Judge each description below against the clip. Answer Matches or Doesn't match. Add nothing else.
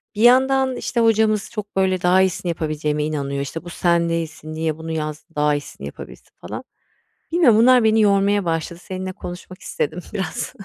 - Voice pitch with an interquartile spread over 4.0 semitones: Matches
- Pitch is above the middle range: Doesn't match